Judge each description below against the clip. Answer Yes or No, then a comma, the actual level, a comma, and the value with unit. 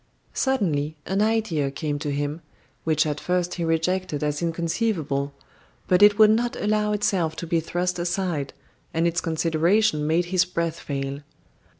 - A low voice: No, medium, 170 Hz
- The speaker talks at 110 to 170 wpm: Yes, average, 155 wpm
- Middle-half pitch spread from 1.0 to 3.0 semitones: No, average, 3.7 semitones